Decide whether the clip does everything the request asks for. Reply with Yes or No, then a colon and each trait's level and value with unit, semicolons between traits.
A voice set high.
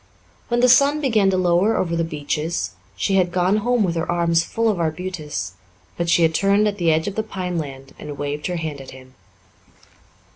No: medium, 175 Hz